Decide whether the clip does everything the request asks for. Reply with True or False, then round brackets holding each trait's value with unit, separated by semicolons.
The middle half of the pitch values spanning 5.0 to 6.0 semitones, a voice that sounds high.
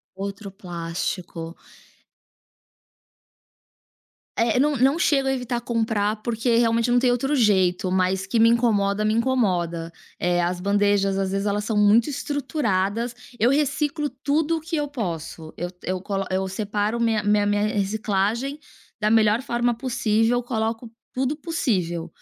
False (4.0 semitones; 220 Hz)